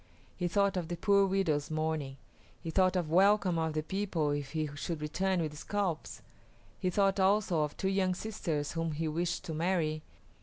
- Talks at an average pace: Yes, average, 185 wpm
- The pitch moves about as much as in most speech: Yes, average, 3.6 semitones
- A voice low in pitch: No, medium, 170 Hz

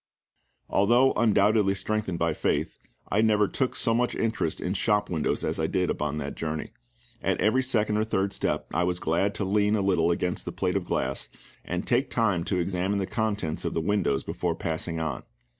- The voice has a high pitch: No, low, 100 Hz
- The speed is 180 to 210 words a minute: Yes, average, 190 wpm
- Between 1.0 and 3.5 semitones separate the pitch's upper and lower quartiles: No, average, 4.2 semitones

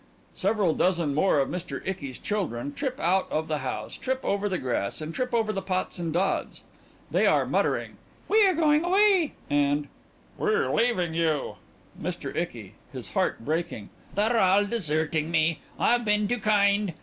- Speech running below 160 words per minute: No, average, 170 wpm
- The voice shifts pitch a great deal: Yes, wide, 6.3 semitones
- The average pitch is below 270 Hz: Yes, high, 190 Hz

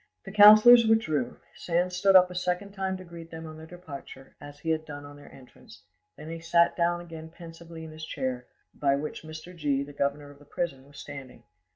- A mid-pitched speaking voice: Yes, medium, 160 Hz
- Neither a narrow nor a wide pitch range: Yes, average, 3.6 semitones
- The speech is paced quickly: Yes, fast, 215 wpm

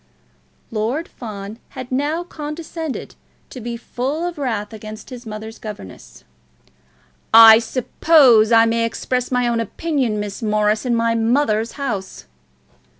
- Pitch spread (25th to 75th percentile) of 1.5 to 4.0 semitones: Yes, average, 3.7 semitones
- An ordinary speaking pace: No, slow, 130 wpm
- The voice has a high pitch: Yes, high, 230 Hz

